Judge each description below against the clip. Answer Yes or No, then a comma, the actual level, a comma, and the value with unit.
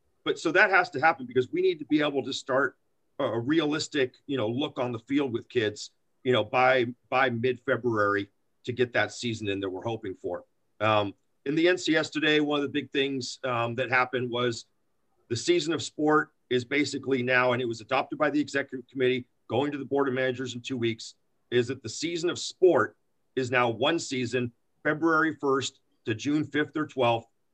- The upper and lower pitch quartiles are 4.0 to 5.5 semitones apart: No, average, 3.3 semitones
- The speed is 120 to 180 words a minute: No, fast, 205 wpm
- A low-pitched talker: Yes, low, 130 Hz